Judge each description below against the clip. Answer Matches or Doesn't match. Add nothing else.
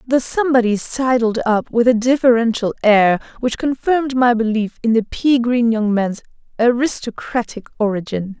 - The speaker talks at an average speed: Matches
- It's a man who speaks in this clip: Doesn't match